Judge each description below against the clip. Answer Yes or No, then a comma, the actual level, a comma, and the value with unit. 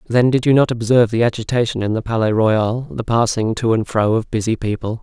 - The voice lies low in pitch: Yes, low, 115 Hz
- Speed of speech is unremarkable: No, fast, 225 wpm